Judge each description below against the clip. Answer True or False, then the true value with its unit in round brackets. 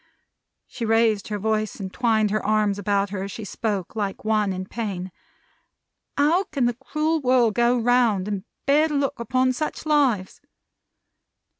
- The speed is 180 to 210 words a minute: False (160 wpm)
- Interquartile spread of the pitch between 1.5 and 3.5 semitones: False (3.9 semitones)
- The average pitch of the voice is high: True (225 Hz)